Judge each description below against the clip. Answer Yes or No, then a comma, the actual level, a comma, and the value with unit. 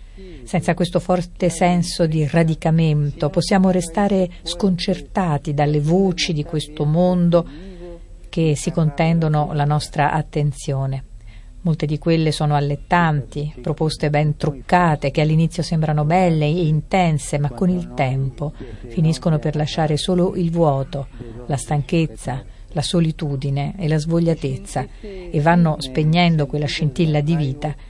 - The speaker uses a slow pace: No, average, 125 wpm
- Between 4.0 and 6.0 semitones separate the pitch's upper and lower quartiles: No, average, 2.9 semitones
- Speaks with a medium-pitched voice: Yes, medium, 155 Hz